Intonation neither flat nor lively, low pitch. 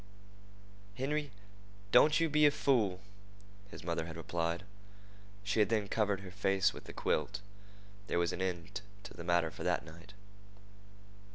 Yes: average, 4.3 semitones; very low, 95 Hz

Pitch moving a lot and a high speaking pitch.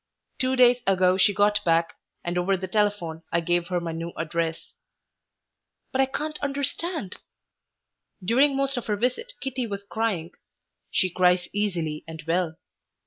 Yes: wide, 6.4 semitones; high, 195 Hz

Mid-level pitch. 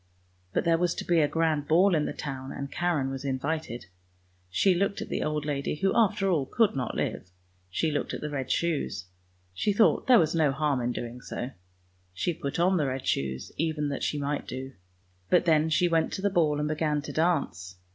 Yes: medium, 150 Hz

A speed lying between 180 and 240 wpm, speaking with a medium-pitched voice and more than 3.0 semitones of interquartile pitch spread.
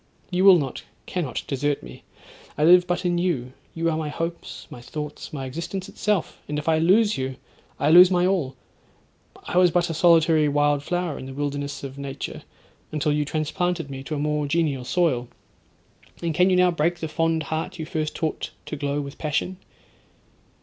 Yes: average, 185 wpm; medium, 155 Hz; average, 3.5 semitones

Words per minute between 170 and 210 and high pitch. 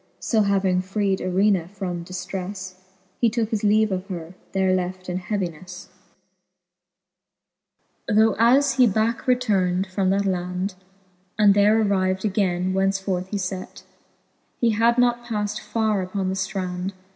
No: average, 145 wpm; high, 195 Hz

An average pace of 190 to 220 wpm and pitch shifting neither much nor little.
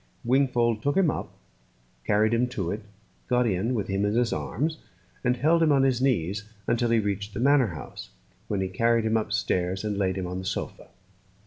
Yes: average, 200 wpm; average, 4.0 semitones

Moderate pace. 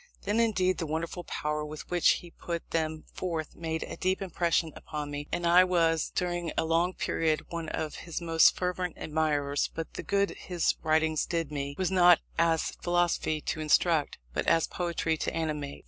Yes: average, 180 wpm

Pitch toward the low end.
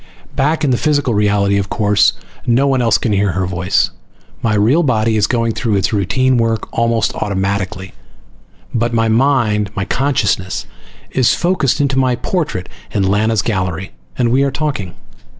Yes: low, 115 Hz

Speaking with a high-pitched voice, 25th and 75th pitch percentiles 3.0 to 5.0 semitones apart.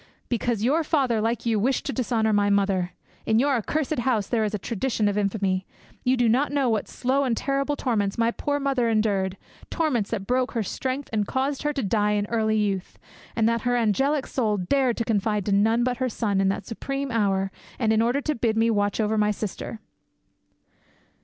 Yes: high, 225 Hz; average, 3.8 semitones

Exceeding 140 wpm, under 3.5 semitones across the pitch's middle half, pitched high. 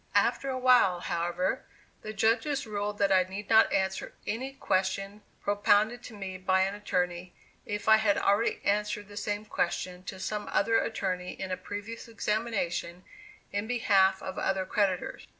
Yes: average, 160 wpm; narrow, 2.5 semitones; high, 205 Hz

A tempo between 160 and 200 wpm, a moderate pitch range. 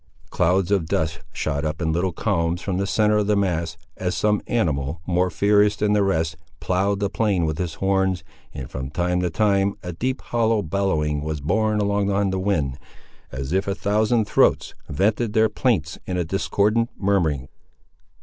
Yes: average, 180 wpm; average, 4.2 semitones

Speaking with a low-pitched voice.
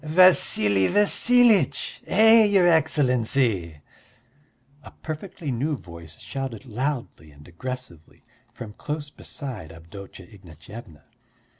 Yes: low, 125 Hz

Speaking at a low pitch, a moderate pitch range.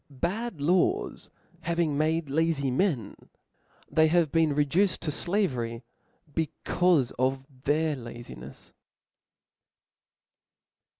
No: medium, 155 Hz; average, 4.1 semitones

